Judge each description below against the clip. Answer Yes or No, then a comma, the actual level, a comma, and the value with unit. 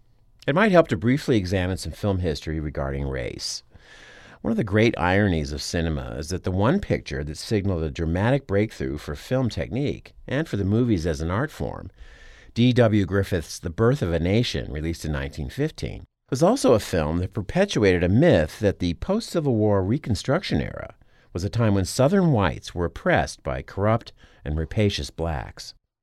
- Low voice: Yes, low, 100 Hz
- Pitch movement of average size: No, wide, 6.0 semitones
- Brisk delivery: No, average, 180 wpm